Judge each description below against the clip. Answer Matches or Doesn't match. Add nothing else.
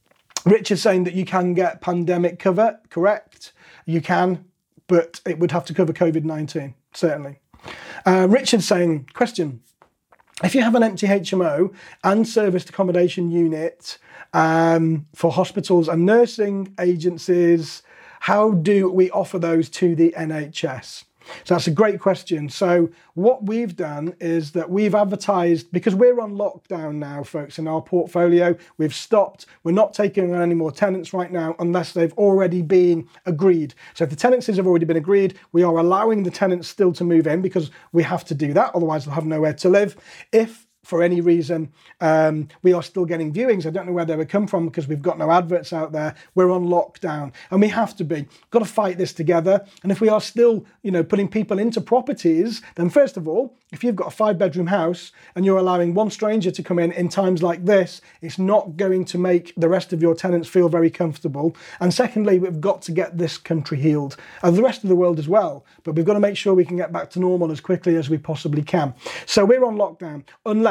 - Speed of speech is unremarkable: Doesn't match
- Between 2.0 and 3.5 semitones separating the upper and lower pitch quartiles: Matches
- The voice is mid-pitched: Matches